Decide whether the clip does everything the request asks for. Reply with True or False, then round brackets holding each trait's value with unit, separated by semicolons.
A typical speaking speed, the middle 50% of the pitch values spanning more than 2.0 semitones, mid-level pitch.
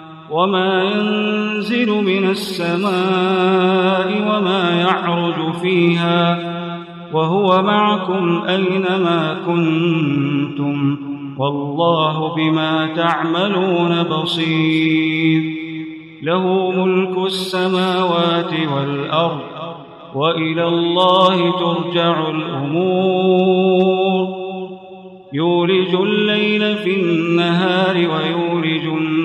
False (55 wpm; 2.6 semitones; 175 Hz)